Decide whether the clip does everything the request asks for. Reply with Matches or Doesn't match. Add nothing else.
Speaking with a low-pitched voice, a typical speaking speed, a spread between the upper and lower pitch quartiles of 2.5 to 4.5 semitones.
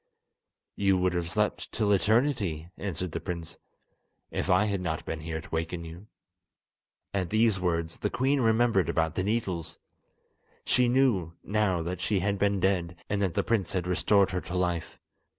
Matches